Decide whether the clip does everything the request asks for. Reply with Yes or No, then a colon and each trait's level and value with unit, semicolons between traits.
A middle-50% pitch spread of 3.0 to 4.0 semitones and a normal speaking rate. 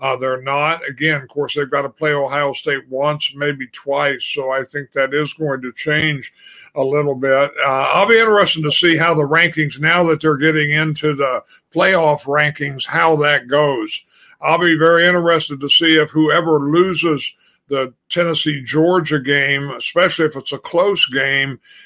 No: narrow, 2.6 semitones; average, 180 wpm